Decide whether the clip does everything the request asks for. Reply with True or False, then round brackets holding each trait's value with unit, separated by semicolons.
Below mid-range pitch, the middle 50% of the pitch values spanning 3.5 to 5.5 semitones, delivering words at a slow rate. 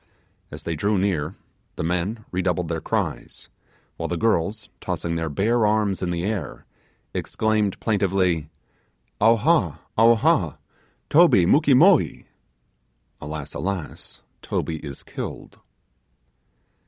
True (95 Hz; 4.8 semitones; 110 wpm)